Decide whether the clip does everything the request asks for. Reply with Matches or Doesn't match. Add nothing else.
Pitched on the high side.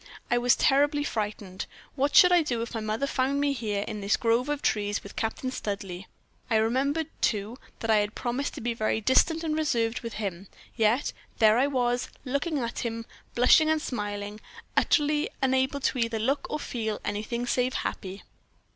Matches